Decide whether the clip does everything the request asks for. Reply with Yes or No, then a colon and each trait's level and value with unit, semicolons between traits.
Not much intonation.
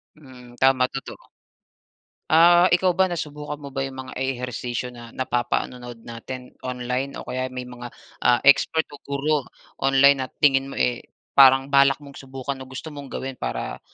Yes: narrow, 2.0 semitones